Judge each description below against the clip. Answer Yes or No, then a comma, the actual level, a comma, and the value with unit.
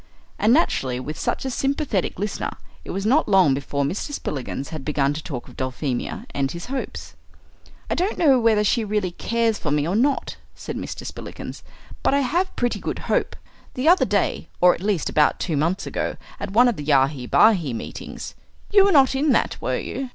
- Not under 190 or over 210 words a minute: Yes, average, 200 wpm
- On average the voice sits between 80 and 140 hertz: No, high, 200 Hz